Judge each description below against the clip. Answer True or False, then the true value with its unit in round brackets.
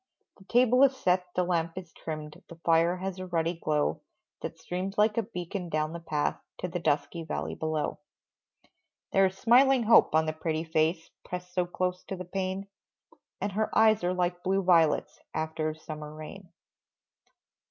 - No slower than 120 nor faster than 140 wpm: False (175 wpm)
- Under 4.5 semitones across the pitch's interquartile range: True (3.2 semitones)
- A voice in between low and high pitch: True (180 Hz)